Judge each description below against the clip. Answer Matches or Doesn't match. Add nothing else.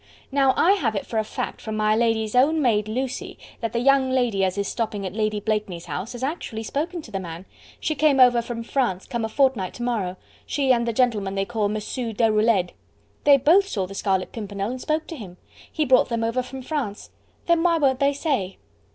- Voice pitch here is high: Matches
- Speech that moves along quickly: Matches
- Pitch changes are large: Doesn't match